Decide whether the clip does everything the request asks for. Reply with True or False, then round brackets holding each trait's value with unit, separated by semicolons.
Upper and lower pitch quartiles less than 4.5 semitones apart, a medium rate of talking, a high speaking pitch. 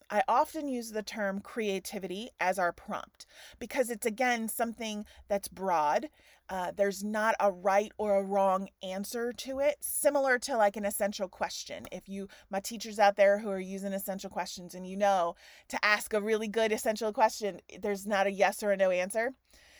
True (2.7 semitones; 185 wpm; 205 Hz)